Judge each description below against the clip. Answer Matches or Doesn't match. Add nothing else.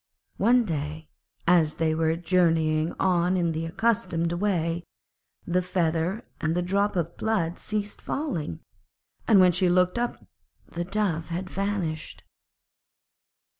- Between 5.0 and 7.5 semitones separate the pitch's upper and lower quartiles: Doesn't match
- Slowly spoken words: Matches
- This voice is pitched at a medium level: Matches